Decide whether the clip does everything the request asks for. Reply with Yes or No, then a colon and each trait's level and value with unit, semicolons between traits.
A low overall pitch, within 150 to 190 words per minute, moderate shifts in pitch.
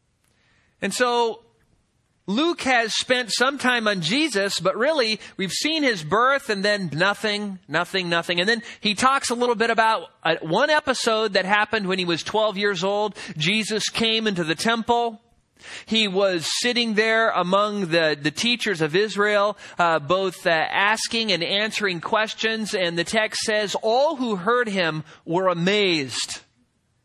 No: high, 210 Hz; average, 155 wpm; average, 3.8 semitones